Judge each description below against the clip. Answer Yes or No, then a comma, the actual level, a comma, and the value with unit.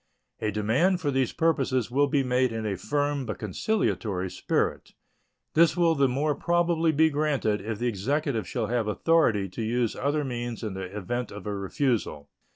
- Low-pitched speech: Yes, low, 125 Hz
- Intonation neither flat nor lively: No, wide, 5.7 semitones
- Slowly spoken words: No, average, 175 wpm